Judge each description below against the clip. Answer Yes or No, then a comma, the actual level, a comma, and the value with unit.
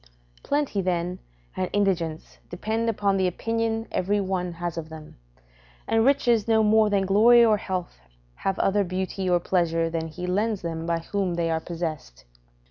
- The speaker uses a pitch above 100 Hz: Yes, medium, 185 Hz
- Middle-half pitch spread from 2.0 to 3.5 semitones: No, average, 3.9 semitones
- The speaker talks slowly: No, average, 165 wpm